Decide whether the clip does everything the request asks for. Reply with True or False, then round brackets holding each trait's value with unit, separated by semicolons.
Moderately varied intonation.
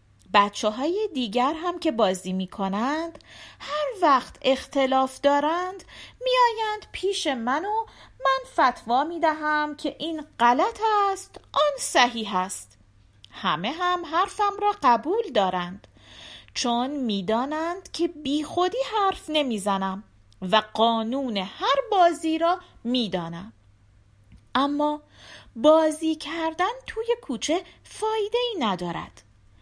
False (8.6 semitones)